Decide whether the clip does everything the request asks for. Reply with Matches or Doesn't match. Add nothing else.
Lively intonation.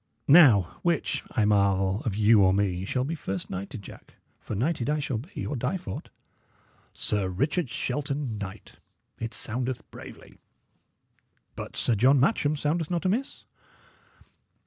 Matches